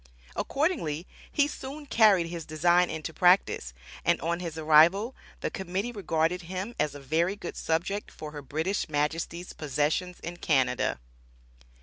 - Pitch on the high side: No, medium, 170 Hz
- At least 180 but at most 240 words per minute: No, average, 140 wpm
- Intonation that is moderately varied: Yes, average, 3.8 semitones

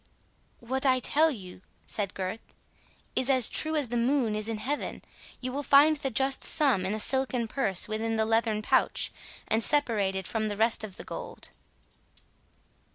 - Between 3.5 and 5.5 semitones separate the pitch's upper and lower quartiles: Yes, average, 4.0 semitones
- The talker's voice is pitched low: No, high, 230 Hz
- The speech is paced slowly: No, average, 170 wpm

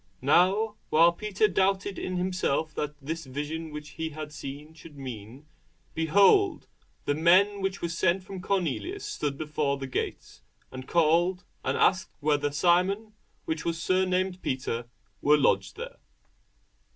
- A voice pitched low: No, medium, 165 Hz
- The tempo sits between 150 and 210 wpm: No, average, 140 wpm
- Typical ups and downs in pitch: Yes, average, 4.0 semitones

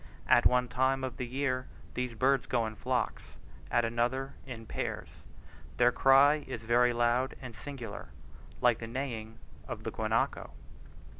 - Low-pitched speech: Yes, low, 125 Hz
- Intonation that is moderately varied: No, narrow, 2.0 semitones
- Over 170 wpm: No, average, 150 wpm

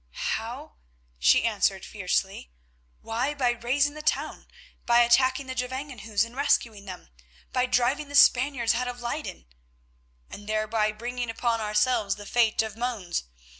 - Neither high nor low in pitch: No, high, 240 Hz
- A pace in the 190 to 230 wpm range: No, average, 140 wpm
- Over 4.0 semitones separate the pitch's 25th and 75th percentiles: No, average, 3.1 semitones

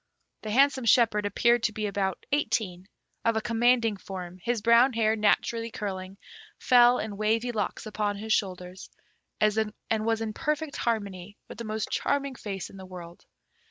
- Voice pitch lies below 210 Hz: No, high, 215 Hz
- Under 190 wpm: Yes, average, 160 wpm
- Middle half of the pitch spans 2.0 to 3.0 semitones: Yes, average, 2.7 semitones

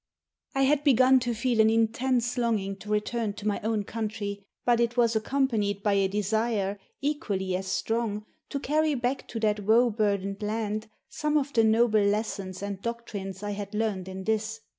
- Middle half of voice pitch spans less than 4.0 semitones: Yes, average, 2.8 semitones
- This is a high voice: Yes, high, 220 Hz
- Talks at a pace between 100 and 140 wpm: No, average, 180 wpm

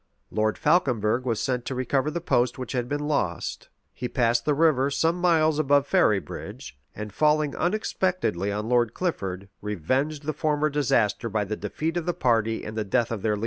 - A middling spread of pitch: No, wide, 5.9 semitones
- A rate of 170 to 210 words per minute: Yes, average, 190 wpm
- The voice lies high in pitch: No, low, 130 Hz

